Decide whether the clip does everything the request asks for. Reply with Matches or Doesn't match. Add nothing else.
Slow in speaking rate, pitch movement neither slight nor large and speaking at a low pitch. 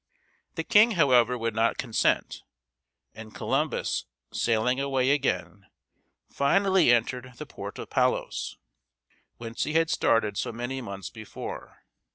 Matches